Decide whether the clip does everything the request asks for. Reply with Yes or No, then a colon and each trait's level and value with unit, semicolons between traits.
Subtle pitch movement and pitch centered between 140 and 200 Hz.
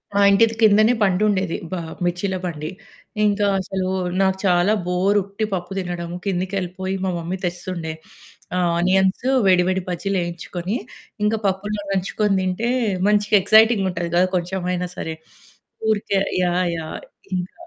Yes: narrow, 2.1 semitones; high, 190 Hz